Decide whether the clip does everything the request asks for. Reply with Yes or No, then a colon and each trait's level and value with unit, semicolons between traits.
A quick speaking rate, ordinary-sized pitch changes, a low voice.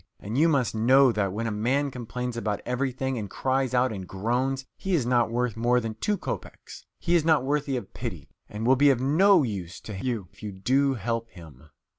Yes: fast, 215 wpm; average, 3.7 semitones; low, 125 Hz